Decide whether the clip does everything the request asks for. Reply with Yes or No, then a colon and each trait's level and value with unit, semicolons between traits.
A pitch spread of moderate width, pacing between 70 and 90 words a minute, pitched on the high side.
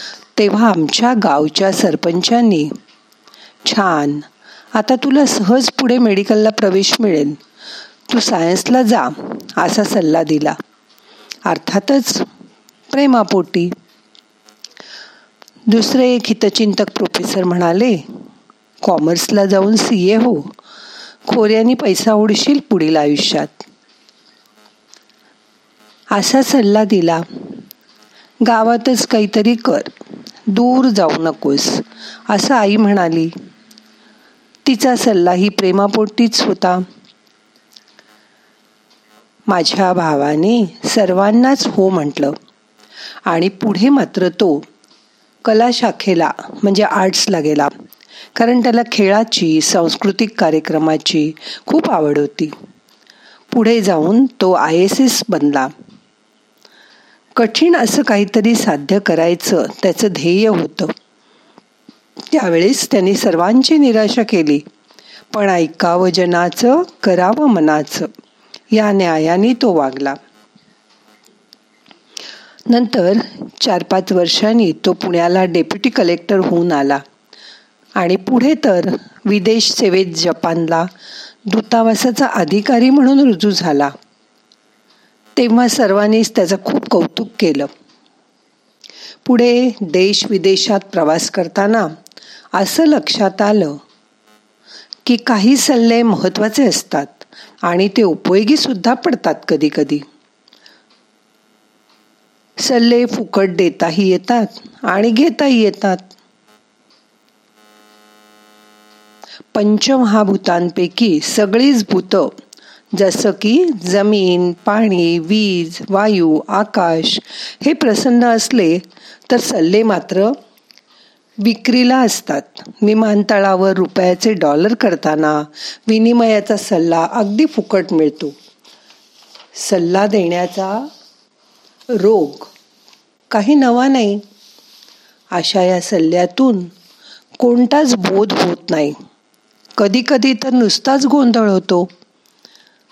No: wide, 5.8 semitones; average, 85 wpm; high, 205 Hz